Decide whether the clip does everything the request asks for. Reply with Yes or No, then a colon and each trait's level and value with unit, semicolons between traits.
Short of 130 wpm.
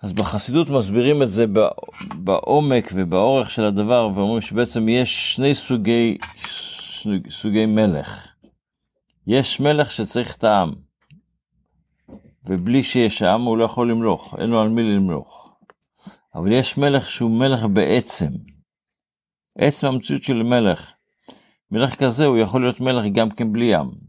No: average, 135 wpm